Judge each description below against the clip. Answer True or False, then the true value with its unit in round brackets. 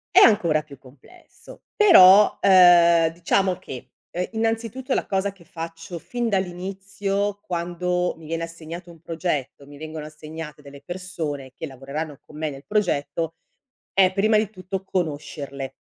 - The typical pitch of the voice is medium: True (170 Hz)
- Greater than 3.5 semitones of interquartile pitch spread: True (3.9 semitones)